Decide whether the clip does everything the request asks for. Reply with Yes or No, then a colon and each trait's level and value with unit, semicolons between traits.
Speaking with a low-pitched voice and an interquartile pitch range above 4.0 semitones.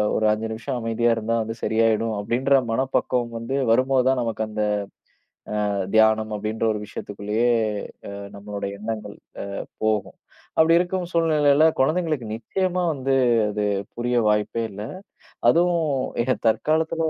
Yes: low, 115 Hz; average, 4.6 semitones